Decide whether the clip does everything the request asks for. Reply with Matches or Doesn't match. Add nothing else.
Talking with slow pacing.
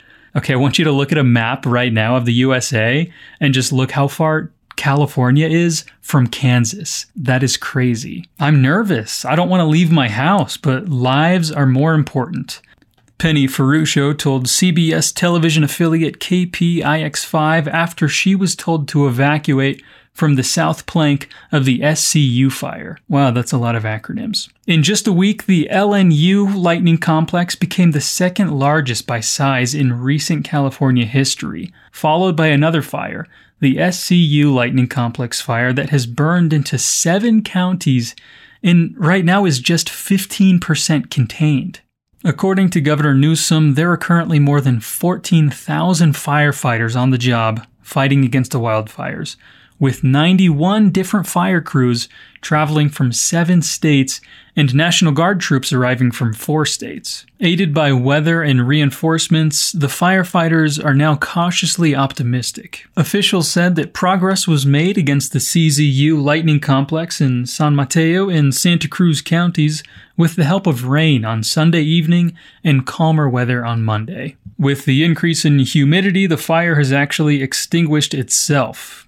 Doesn't match